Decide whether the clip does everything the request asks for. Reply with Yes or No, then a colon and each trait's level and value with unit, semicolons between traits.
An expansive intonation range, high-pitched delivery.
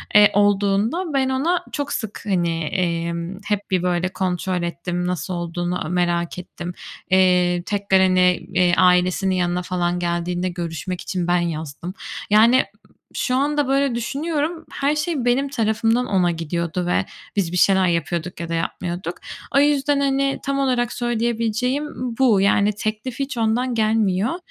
Yes: wide, 5.9 semitones; high, 195 Hz